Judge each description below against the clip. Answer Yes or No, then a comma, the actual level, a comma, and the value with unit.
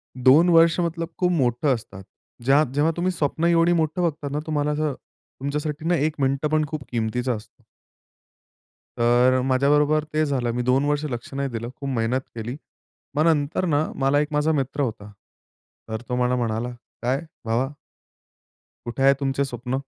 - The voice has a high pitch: No, medium, 140 Hz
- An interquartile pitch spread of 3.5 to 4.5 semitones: Yes, average, 3.8 semitones